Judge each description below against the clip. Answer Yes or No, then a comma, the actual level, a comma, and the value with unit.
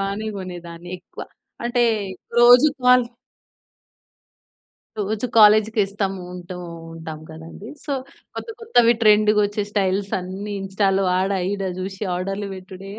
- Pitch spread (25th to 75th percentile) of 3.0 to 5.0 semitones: No, narrow, 2.6 semitones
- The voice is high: Yes, high, 200 Hz